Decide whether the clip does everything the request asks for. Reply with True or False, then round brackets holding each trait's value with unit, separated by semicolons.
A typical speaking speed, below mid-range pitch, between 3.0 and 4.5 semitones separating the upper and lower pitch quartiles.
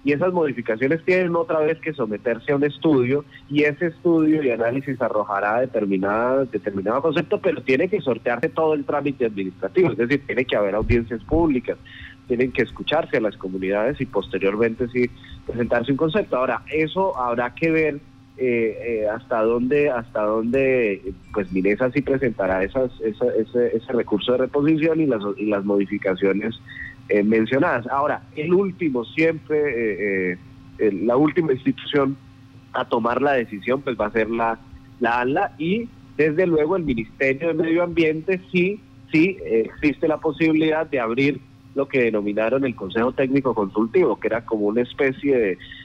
False (165 wpm; 130 Hz; 5.2 semitones)